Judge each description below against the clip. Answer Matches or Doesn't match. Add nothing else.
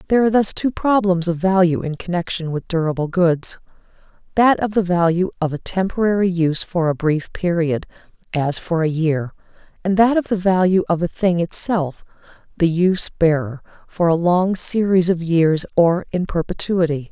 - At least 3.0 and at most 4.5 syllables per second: Doesn't match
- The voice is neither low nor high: Matches